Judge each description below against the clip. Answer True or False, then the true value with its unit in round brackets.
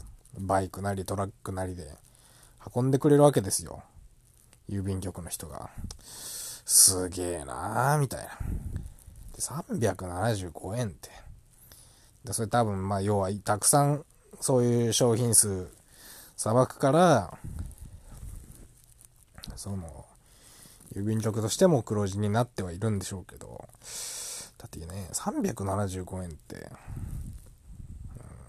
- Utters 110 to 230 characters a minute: True (210 characters per minute)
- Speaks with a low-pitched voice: True (105 Hz)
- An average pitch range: True (4.3 semitones)